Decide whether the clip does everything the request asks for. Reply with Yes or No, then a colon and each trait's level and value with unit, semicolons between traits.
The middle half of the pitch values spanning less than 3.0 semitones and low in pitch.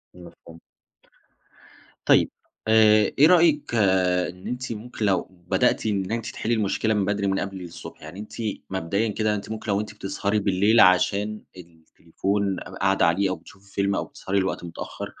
Yes: narrow, 2.5 semitones; low, 100 Hz